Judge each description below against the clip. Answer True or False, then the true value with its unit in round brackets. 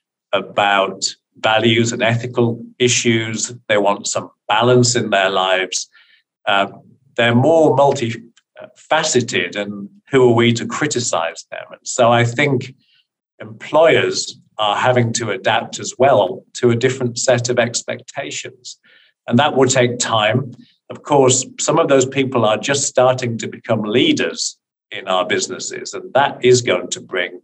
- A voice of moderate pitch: False (120 Hz)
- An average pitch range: False (2.0 semitones)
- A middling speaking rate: True (145 wpm)